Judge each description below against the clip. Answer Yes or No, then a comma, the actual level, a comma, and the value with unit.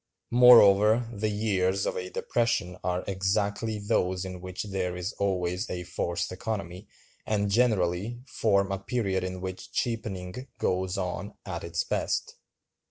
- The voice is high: No, very low, 95 Hz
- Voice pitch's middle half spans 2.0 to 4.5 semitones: Yes, average, 2.8 semitones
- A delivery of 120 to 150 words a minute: Yes, average, 140 wpm